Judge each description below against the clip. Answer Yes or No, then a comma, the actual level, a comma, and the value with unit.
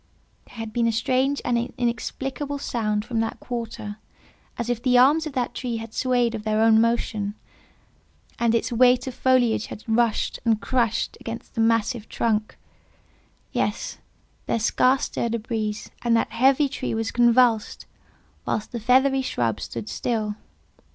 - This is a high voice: Yes, high, 235 Hz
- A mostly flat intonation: Yes, narrow, 2.2 semitones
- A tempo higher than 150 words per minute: Yes, average, 160 wpm